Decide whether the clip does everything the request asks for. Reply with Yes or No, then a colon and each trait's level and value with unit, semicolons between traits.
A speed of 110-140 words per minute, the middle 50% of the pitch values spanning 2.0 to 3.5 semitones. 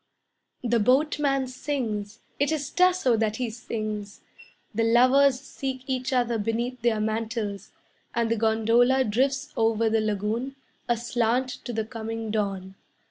Yes: slow, 135 wpm; average, 2.9 semitones